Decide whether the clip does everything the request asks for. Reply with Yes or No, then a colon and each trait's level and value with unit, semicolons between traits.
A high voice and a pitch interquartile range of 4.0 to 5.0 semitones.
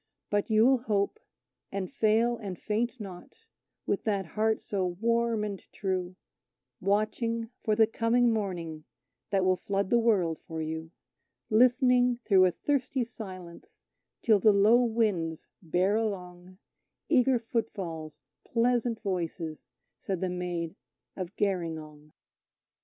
Yes: high, 200 Hz; average, 4.3 semitones